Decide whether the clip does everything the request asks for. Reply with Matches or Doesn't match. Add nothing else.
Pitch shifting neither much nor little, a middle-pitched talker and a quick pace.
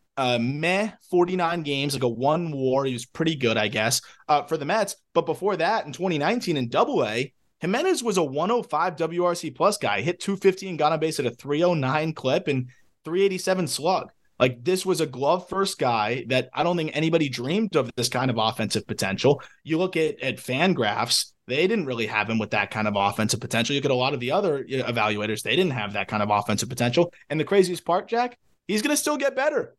Doesn't match